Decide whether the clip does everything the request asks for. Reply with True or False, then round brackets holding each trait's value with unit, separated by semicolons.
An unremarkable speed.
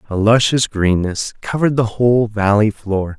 True (150 wpm)